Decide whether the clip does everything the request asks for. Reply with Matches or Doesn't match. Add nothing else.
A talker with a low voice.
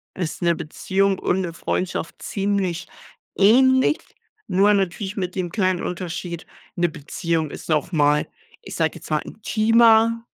Doesn't match